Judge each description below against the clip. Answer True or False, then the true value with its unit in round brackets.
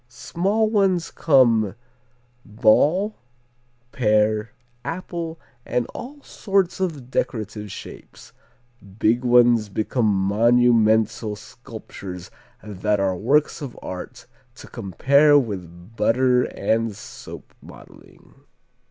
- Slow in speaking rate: True (90 wpm)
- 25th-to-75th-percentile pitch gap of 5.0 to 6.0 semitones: True (5.5 semitones)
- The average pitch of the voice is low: True (115 Hz)